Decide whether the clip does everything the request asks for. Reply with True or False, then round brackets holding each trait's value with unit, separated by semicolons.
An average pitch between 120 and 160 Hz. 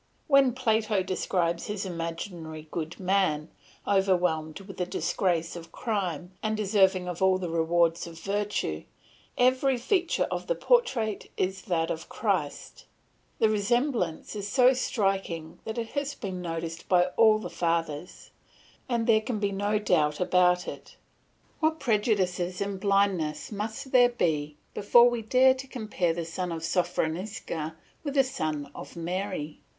False (190 Hz)